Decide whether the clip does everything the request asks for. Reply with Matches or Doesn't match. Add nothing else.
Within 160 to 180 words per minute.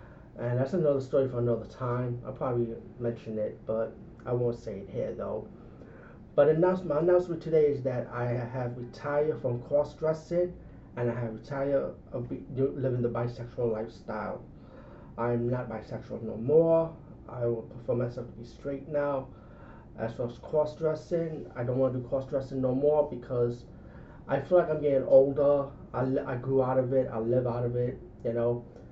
Matches